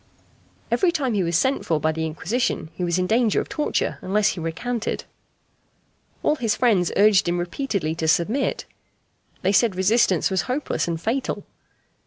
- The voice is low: No, high, 195 Hz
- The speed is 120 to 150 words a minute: No, average, 165 wpm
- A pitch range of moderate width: No, wide, 5.9 semitones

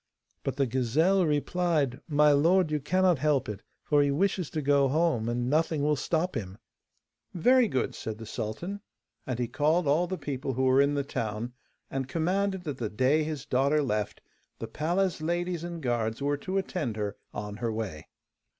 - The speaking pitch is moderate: Yes, medium, 145 Hz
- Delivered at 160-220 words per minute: Yes, average, 185 wpm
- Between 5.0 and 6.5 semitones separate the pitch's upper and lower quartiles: Yes, wide, 5.6 semitones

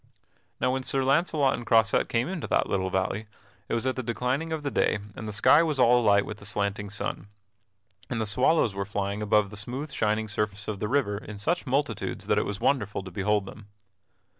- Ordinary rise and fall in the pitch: Yes, average, 4.3 semitones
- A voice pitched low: Yes, low, 110 Hz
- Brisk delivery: Yes, fast, 215 wpm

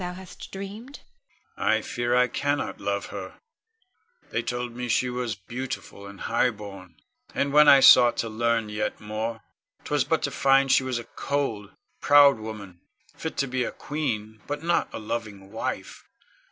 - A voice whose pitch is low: Yes, low, 120 Hz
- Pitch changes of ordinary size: Yes, average, 4.0 semitones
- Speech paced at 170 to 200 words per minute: No, average, 155 wpm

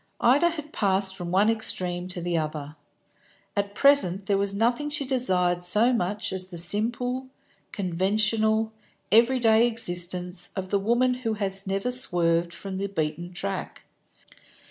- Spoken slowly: No, average, 145 wpm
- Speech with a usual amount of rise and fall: Yes, average, 4.5 semitones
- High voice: Yes, high, 200 Hz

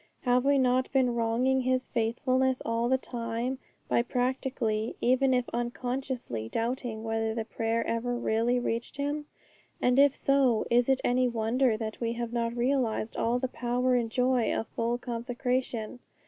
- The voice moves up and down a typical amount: No, narrow, 1.9 semitones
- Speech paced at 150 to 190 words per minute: Yes, average, 160 wpm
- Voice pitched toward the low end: No, high, 245 Hz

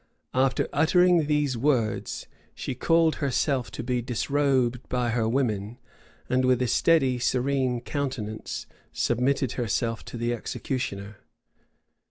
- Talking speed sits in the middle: No, slow, 120 wpm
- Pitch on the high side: No, low, 125 Hz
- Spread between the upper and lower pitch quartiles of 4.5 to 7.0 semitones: No, average, 2.9 semitones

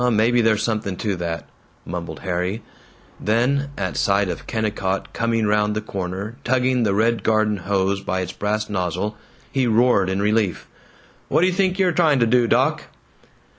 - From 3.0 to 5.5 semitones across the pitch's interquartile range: Yes, average, 3.4 semitones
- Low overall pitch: Yes, low, 105 Hz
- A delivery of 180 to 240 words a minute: No, average, 170 wpm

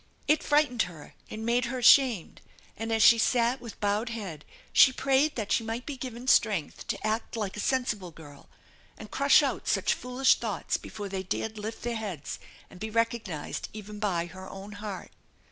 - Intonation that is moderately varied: Yes, average, 3.6 semitones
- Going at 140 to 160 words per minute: No, average, 185 wpm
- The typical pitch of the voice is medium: No, high, 220 Hz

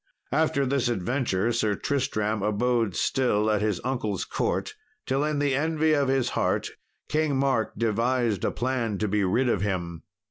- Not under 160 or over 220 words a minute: Yes, average, 165 wpm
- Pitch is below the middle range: Yes, low, 120 Hz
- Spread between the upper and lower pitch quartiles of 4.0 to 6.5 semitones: Yes, average, 4.4 semitones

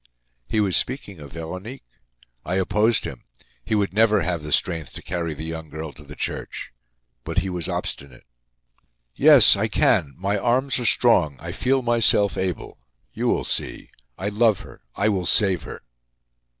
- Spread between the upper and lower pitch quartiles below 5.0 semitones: No, average, 5.3 semitones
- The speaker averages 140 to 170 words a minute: Yes, average, 165 wpm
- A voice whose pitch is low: Yes, very low, 95 Hz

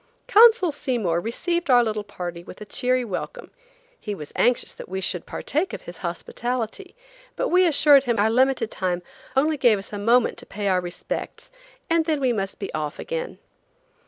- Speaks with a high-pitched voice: Yes, high, 235 Hz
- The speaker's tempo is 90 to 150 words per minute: No, average, 185 wpm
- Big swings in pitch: Yes, wide, 7.3 semitones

